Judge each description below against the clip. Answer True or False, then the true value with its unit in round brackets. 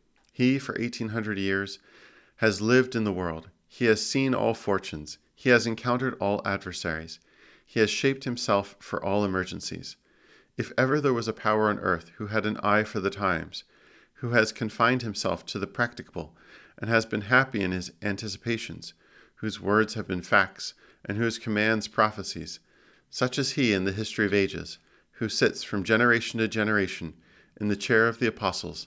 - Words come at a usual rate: True (175 wpm)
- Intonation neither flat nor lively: True (3.0 semitones)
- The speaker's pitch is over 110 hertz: False (105 Hz)